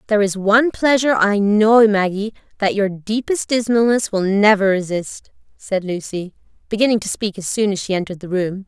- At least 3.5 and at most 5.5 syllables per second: Yes, 5.4 syllables/s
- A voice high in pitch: Yes, high, 205 Hz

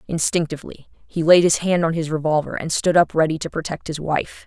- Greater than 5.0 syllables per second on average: Yes, 5.6 syllables/s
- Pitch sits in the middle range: Yes, medium, 160 Hz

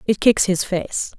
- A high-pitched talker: Yes, high, 195 Hz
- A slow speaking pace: No, average, 200 wpm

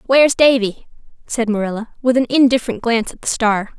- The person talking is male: No, female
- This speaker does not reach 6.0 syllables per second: No, 6.1 syllables/s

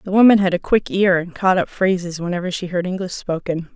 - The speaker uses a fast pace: Yes, fast, 240 wpm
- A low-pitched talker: No, medium, 185 Hz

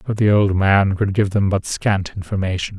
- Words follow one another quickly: Yes, fast, 215 wpm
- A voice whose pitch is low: Yes, low, 100 Hz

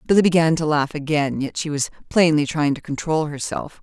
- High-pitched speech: No, medium, 155 Hz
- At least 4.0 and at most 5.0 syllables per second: No, 5.5 syllables/s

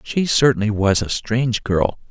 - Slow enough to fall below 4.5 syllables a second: No, 4.7 syllables/s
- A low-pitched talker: Yes, low, 115 Hz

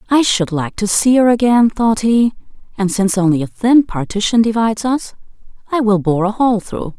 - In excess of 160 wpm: Yes, average, 200 wpm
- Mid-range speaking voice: No, high, 215 Hz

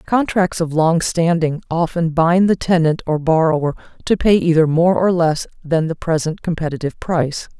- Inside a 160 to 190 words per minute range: Yes, average, 165 wpm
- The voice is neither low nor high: Yes, medium, 165 Hz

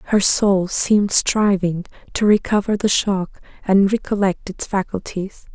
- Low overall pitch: No, high, 195 Hz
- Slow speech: Yes, slow, 130 wpm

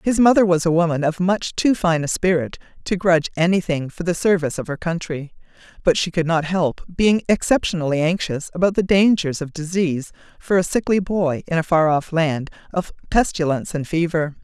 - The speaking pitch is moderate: Yes, medium, 170 Hz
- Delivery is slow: No, average, 190 wpm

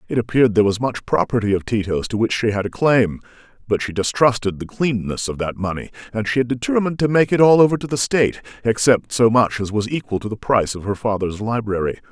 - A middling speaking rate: No, fast, 235 wpm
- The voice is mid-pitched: No, low, 115 Hz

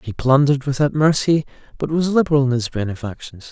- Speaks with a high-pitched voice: No, medium, 140 Hz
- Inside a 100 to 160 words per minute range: No, average, 170 wpm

